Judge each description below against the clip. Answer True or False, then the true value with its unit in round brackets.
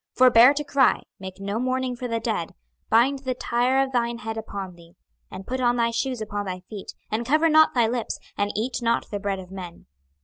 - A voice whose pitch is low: False (235 Hz)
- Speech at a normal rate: False (225 wpm)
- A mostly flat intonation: False (4.0 semitones)